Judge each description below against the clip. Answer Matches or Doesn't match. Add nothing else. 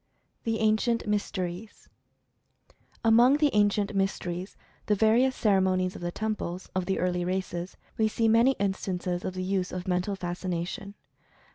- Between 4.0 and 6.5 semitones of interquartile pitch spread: Doesn't match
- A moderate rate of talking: Matches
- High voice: Matches